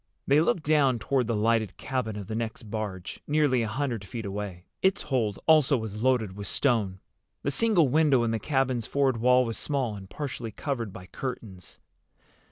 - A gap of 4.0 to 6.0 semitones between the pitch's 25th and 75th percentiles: Yes, average, 4.5 semitones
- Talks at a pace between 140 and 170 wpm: No, average, 180 wpm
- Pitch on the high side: No, low, 120 Hz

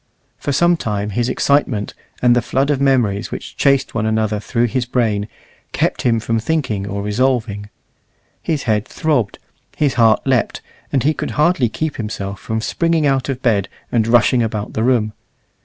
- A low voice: Yes, low, 120 Hz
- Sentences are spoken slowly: No, average, 175 wpm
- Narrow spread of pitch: No, average, 4.1 semitones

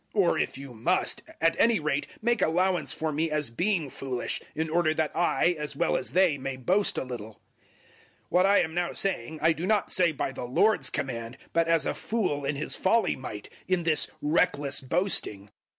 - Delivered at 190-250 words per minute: Yes, average, 200 wpm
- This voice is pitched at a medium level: Yes, medium, 160 Hz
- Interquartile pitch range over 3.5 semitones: Yes, average, 4.8 semitones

